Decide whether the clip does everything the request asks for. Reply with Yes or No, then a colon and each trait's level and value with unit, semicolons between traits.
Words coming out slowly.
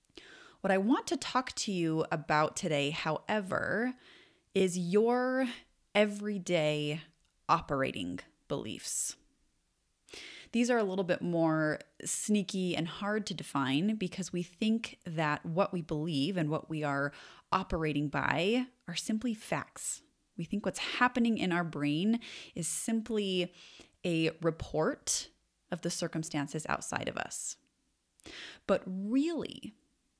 Yes: slow, 120 wpm